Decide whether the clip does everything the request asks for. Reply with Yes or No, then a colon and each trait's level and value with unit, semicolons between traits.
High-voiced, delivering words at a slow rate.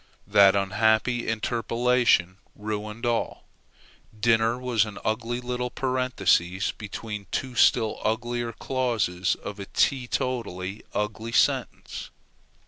No: low, 115 Hz; slow, 105 wpm